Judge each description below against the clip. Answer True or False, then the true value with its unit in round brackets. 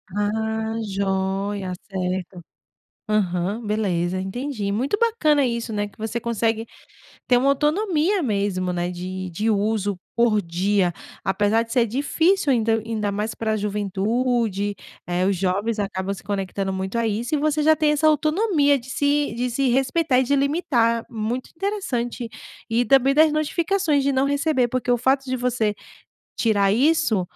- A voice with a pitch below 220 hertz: False (230 Hz)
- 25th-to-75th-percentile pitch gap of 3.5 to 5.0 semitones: False (5.5 semitones)